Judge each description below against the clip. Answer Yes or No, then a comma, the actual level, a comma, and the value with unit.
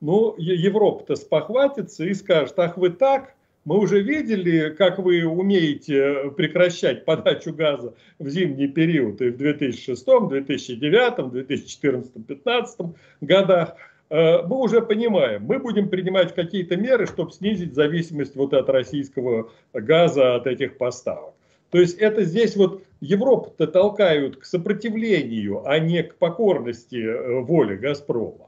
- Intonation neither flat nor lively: No, wide, 5.7 semitones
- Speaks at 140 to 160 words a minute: No, average, 125 wpm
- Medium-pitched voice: Yes, medium, 170 Hz